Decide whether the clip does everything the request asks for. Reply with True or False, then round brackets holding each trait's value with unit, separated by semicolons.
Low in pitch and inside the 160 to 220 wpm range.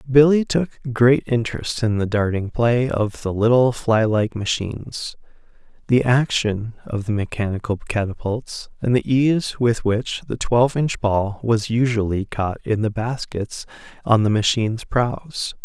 False (115 Hz; 145 wpm)